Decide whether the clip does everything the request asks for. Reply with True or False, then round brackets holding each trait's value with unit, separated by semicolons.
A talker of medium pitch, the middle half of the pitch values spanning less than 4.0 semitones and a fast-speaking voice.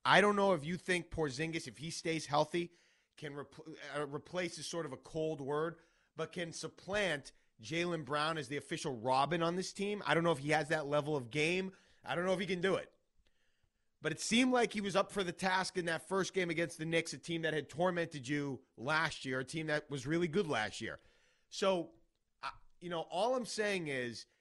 True (160 Hz; 3.4 semitones; 225 wpm)